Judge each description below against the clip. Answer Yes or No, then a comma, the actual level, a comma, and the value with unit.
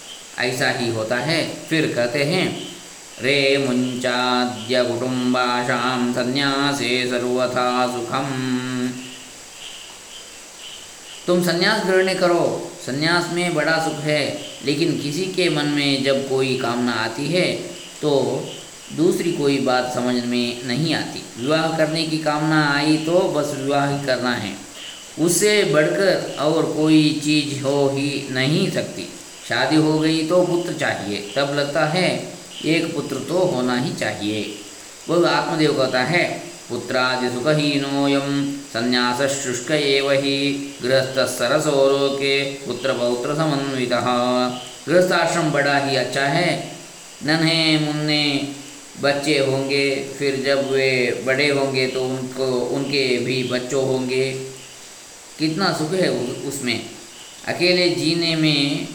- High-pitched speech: No, medium, 140 Hz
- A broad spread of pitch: No, average, 3.7 semitones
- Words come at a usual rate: No, fast, 120 wpm